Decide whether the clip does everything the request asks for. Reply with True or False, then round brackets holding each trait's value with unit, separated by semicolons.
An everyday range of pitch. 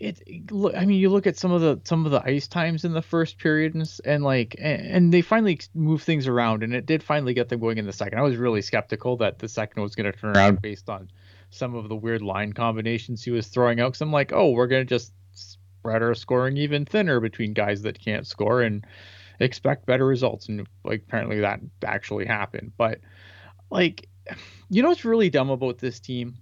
False (5.8 semitones)